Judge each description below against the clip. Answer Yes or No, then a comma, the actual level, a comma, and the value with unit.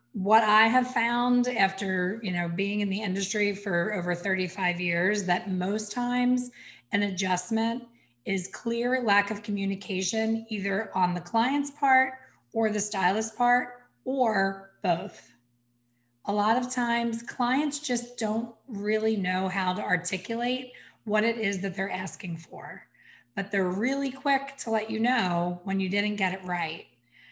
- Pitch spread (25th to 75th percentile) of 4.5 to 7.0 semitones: No, average, 4.0 semitones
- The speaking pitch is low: No, high, 205 Hz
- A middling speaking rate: Yes, average, 150 wpm